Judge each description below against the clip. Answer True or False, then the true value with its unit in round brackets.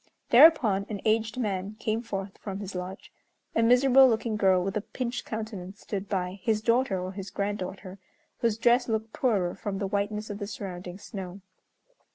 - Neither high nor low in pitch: False (205 Hz)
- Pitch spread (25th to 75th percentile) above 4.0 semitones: False (2.8 semitones)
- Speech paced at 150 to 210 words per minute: True (175 wpm)